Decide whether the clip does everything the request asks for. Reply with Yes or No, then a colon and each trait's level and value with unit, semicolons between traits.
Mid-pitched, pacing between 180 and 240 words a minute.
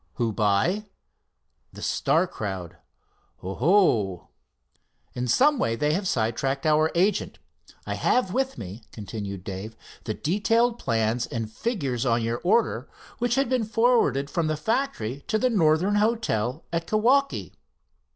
No: medium, 155 Hz; slow, 135 wpm